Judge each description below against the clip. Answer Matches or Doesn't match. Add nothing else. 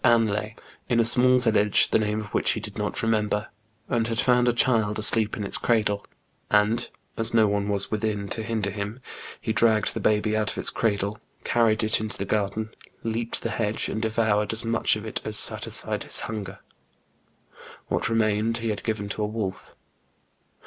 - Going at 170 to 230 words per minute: Matches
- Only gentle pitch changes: Matches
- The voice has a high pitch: Doesn't match